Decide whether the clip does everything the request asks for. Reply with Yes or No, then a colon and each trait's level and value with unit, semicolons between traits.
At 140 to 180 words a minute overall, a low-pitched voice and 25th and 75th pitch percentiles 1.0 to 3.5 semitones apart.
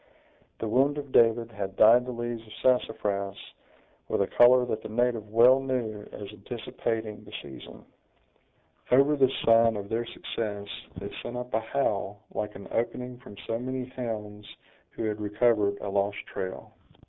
Yes: average, 160 wpm; low, 115 Hz; average, 3.0 semitones